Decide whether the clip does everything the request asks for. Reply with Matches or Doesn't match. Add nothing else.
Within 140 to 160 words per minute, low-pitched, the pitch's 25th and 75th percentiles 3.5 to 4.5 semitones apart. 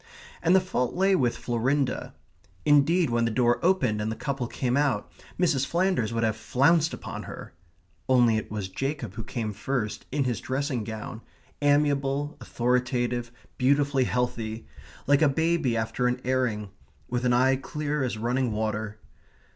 Matches